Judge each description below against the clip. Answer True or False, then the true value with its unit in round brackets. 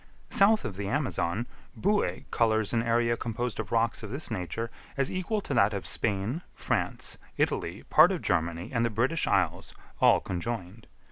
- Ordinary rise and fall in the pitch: True (4.4 semitones)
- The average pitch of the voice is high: False (115 Hz)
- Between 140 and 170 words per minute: True (165 wpm)